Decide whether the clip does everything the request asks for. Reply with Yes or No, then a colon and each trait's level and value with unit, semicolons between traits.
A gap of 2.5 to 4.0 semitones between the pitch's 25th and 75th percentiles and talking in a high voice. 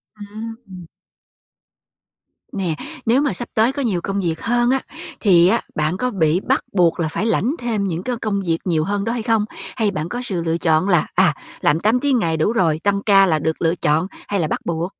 No: average, 5.3 semitones; high, 195 Hz